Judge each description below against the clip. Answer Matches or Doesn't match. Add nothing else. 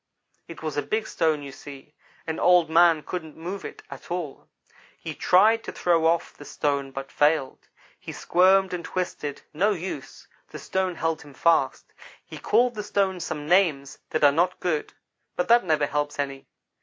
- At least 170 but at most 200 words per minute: Matches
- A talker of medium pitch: Matches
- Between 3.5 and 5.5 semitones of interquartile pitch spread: Matches